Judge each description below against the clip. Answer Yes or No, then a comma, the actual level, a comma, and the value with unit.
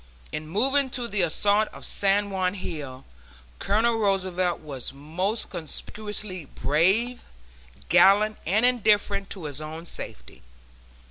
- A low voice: No, high, 195 Hz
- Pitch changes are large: No, average, 4.7 semitones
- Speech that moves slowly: Yes, slow, 120 wpm